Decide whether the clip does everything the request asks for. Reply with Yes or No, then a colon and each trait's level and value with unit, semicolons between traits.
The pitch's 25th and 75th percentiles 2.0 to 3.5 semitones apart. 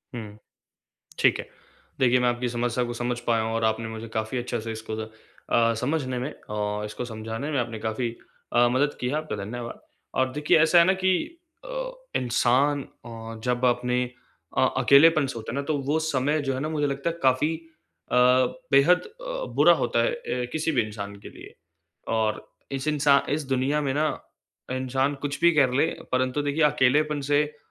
No: average, 4.1 semitones